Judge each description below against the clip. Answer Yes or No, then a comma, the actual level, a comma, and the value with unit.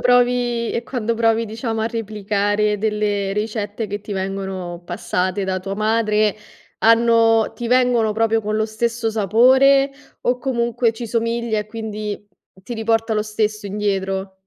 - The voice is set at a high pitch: Yes, high, 220 Hz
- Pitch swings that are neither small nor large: No, narrow, 2.1 semitones